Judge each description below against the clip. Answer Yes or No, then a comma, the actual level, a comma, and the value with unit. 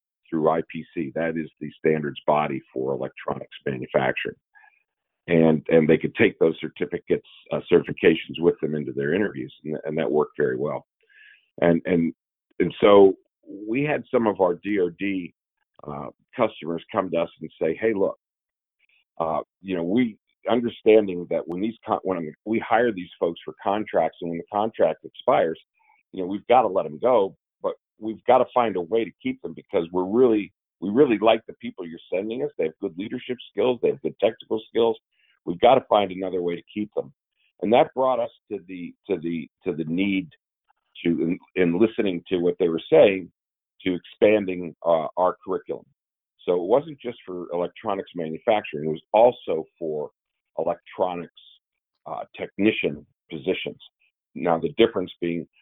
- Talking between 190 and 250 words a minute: No, average, 175 wpm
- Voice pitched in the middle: No, very low, 90 Hz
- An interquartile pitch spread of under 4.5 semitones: No, wide, 5.4 semitones